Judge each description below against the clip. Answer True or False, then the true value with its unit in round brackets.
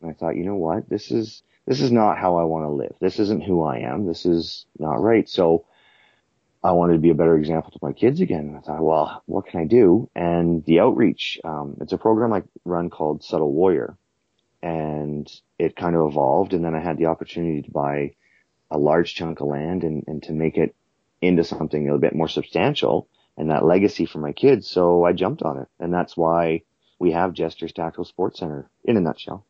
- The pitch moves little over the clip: True (2.2 semitones)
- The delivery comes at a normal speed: False (225 wpm)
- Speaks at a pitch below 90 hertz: True (80 Hz)